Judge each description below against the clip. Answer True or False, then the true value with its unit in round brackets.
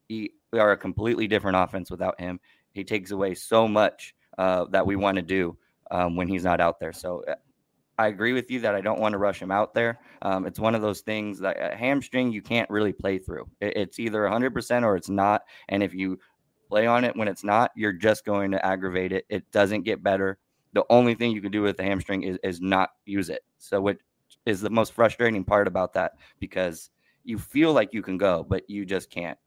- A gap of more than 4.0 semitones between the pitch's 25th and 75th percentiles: False (2.9 semitones)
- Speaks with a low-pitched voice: True (100 Hz)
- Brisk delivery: True (225 wpm)